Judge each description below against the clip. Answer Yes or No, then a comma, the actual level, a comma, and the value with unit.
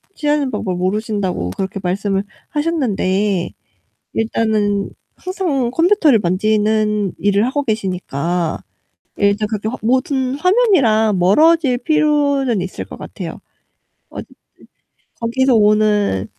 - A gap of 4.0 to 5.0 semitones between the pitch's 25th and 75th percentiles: No, wide, 5.4 semitones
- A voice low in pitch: No, high, 215 Hz